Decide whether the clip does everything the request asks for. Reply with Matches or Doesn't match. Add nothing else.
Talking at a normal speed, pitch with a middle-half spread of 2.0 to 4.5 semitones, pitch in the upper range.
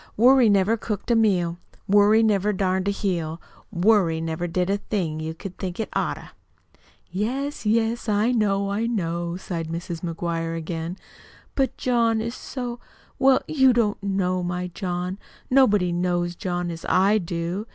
Matches